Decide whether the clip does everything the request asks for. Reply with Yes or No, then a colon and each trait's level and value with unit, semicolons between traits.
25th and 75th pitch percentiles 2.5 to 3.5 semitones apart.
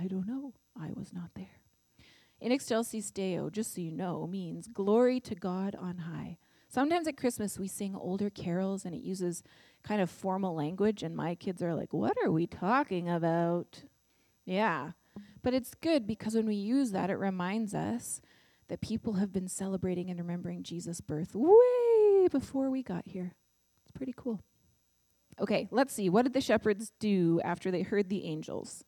No: average, 4.3 semitones